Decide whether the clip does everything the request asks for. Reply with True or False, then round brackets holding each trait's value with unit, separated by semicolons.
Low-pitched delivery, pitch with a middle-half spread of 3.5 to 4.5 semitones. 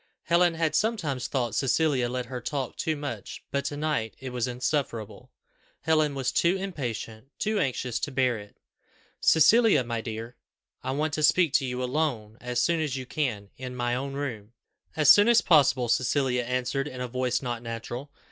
True (130 Hz; 3.9 semitones)